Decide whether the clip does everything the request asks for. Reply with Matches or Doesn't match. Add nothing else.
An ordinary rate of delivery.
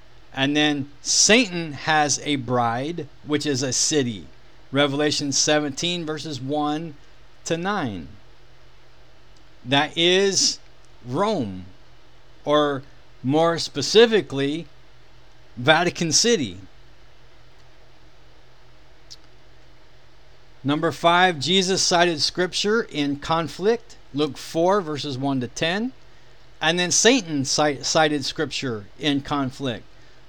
Doesn't match